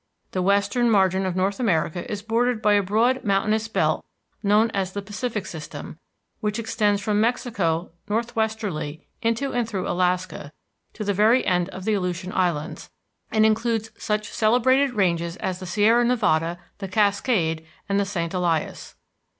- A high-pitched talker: Yes, high, 205 Hz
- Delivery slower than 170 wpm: Yes, average, 155 wpm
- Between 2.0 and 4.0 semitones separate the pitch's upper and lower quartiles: Yes, average, 3.4 semitones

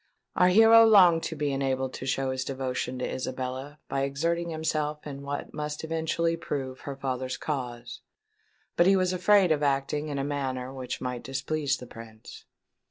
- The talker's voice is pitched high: No, medium, 140 Hz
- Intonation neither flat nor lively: Yes, average, 3.5 semitones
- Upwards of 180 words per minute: No, average, 170 wpm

